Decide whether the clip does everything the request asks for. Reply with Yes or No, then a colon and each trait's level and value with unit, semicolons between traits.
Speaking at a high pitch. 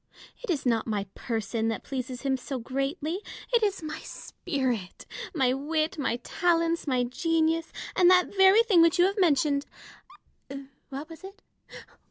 Yes: very high, 300 Hz